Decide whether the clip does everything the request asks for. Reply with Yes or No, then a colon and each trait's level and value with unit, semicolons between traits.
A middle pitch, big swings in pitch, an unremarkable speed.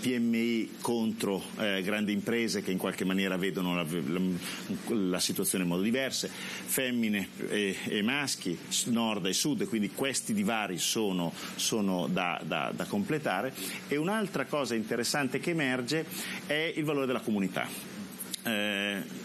No: low, 110 Hz; wide, 5.7 semitones; average, 145 wpm